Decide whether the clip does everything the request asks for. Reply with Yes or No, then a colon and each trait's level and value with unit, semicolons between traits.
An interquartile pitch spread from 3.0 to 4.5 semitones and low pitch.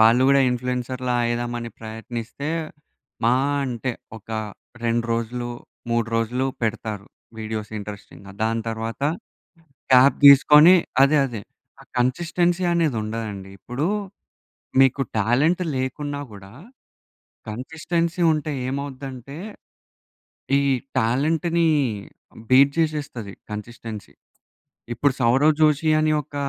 Yes: average, 4.1 semitones; low, 125 Hz